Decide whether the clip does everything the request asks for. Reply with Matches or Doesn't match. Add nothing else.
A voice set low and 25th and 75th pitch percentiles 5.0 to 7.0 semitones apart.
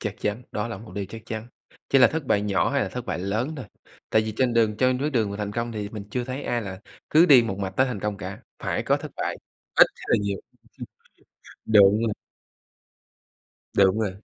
Doesn't match